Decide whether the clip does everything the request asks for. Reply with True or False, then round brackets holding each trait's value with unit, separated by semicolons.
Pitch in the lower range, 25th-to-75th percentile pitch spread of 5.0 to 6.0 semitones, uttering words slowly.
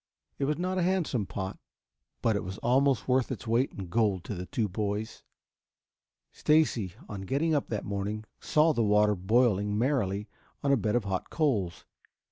False (110 Hz; 5.3 semitones; 175 wpm)